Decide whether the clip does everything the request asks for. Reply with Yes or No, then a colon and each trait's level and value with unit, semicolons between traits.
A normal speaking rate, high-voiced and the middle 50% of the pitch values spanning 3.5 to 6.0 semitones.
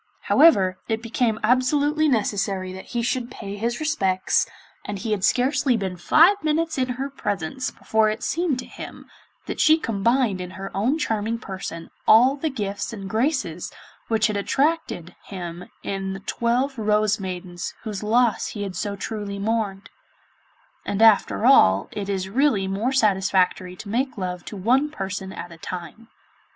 Yes: average, 165 wpm; high, 215 Hz; average, 4.9 semitones